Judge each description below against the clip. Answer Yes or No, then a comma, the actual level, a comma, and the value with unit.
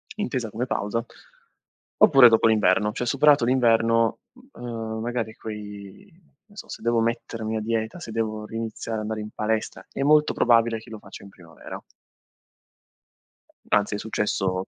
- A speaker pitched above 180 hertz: No, low, 115 Hz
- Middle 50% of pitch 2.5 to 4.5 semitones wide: No, narrow, 1.9 semitones